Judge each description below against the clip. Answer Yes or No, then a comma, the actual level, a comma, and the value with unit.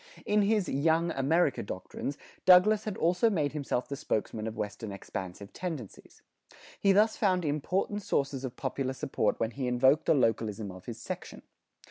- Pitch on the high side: No, medium, 140 Hz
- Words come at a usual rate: Yes, average, 160 wpm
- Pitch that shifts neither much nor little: No, wide, 7.7 semitones